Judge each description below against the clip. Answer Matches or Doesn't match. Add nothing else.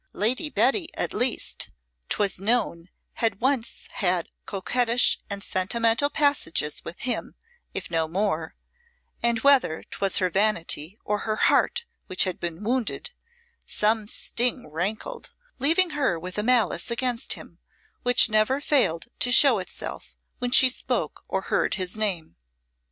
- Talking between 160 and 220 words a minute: Doesn't match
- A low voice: Doesn't match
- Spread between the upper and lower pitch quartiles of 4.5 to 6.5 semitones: Matches